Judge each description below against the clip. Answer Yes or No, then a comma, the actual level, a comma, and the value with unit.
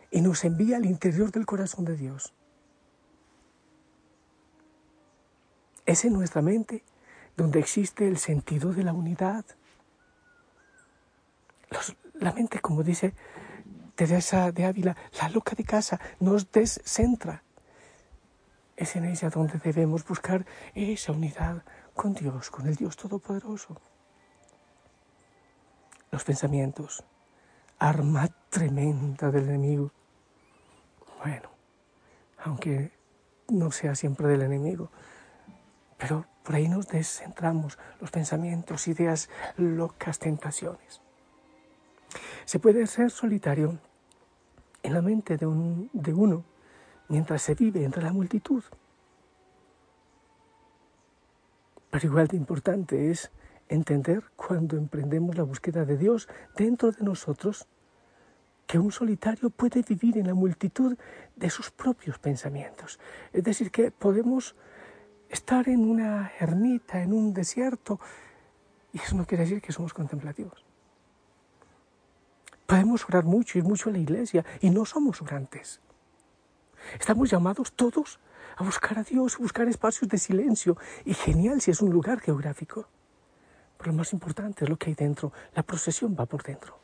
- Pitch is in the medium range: Yes, medium, 175 Hz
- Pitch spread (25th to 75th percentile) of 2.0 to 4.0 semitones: No, average, 5.2 semitones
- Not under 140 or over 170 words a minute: No, slow, 125 wpm